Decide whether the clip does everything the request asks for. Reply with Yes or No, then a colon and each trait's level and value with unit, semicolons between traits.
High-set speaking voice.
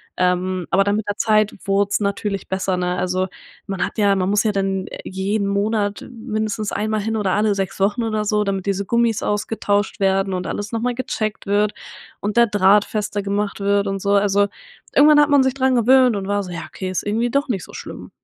Yes: high, 205 Hz